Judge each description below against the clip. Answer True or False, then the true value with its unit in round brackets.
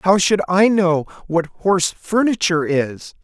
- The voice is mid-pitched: True (180 Hz)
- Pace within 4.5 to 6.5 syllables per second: False (4.2 syllables/s)